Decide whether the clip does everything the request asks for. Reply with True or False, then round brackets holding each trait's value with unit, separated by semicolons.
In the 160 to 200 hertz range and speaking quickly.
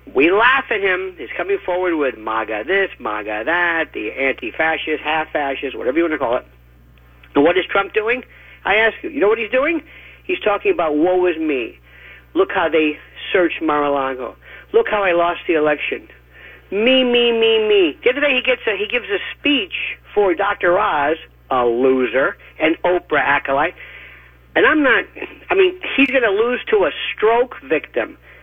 False (190 Hz; 180 wpm)